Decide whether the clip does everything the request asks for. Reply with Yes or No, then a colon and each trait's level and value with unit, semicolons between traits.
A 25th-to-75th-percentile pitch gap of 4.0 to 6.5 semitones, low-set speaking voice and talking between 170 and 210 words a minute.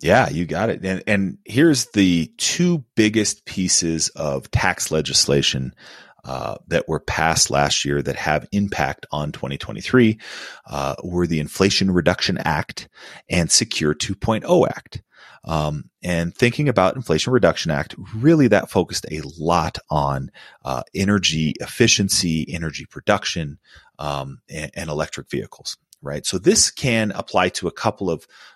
No: wide, 5.5 semitones; very low, 90 Hz; average, 140 wpm